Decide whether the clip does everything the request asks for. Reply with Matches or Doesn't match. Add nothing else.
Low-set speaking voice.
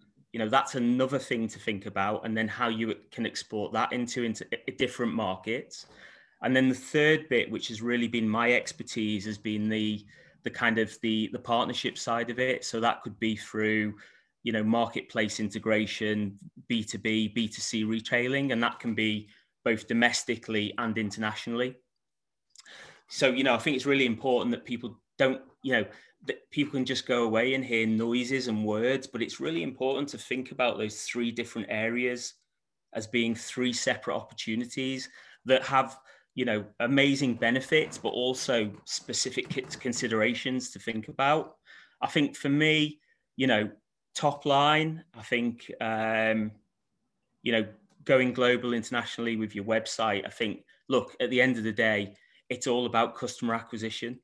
Matches